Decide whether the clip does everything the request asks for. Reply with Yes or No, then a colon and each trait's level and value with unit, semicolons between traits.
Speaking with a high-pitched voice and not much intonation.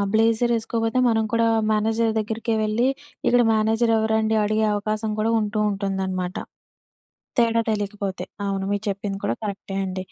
Yes: high, 215 Hz; narrow, 1.9 semitones